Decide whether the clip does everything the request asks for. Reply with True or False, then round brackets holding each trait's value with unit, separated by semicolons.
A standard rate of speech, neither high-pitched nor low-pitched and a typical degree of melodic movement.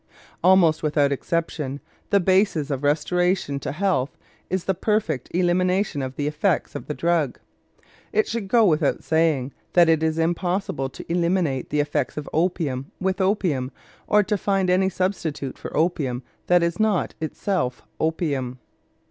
True (150 wpm; 165 Hz; 4.4 semitones)